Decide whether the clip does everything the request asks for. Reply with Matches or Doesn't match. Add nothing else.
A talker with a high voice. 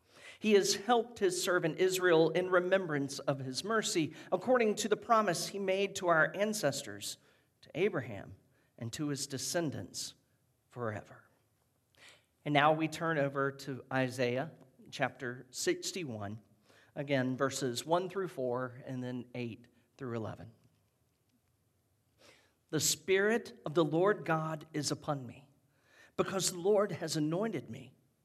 Doesn't match